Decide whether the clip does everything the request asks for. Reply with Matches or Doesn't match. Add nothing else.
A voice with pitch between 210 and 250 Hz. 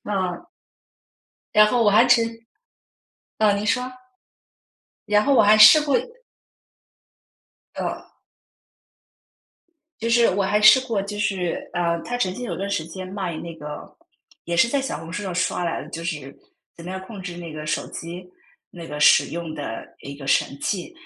Doesn't match